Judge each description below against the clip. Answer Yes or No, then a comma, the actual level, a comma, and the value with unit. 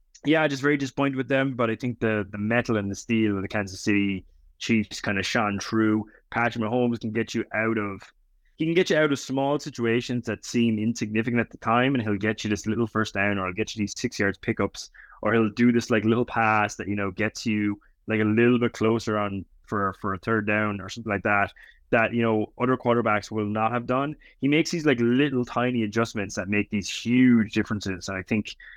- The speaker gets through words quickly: Yes, fast, 235 wpm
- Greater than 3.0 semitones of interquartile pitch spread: No, narrow, 2.6 semitones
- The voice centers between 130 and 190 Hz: No, low, 110 Hz